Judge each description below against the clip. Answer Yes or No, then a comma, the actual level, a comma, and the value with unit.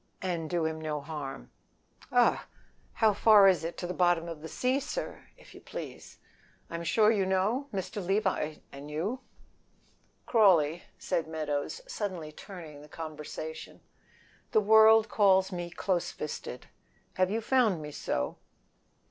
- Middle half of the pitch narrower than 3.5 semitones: No, average, 4.8 semitones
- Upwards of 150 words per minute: No, average, 145 wpm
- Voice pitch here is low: No, medium, 180 Hz